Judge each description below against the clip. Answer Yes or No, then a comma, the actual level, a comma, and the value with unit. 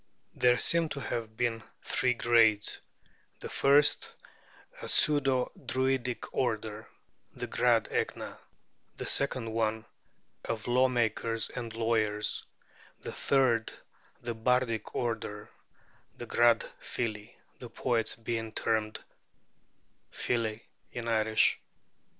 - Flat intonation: Yes, narrow, 2.0 semitones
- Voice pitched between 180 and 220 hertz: No, low, 115 Hz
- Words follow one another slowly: Yes, slow, 105 wpm